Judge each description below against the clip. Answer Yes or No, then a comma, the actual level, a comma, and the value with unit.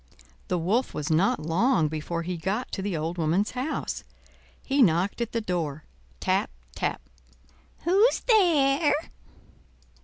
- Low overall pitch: No, medium, 185 Hz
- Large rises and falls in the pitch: Yes, wide, 8.4 semitones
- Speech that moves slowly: Yes, slow, 125 wpm